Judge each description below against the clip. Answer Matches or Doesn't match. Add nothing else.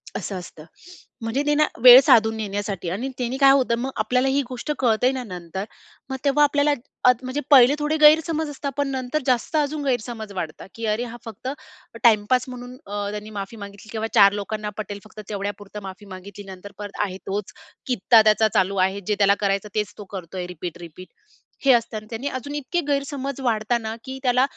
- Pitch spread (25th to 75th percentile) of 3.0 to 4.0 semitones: Doesn't match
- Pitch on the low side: Doesn't match